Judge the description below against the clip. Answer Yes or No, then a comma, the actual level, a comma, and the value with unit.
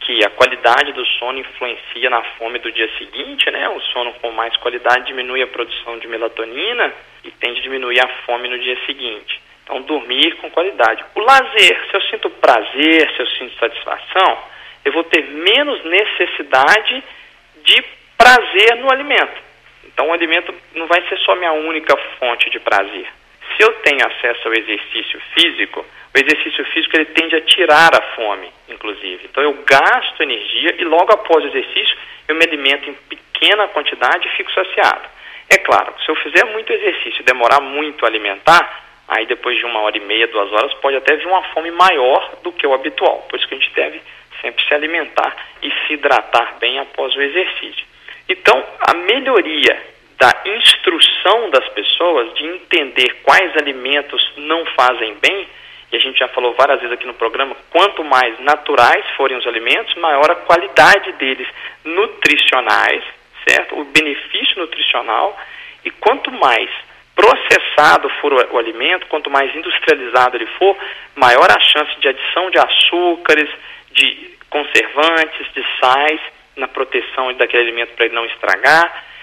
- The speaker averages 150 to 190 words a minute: Yes, average, 165 wpm